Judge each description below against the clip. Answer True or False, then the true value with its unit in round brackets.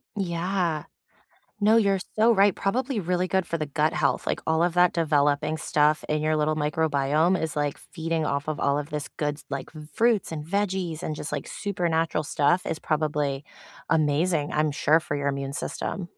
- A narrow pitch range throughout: False (3.3 semitones)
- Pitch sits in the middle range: True (160 Hz)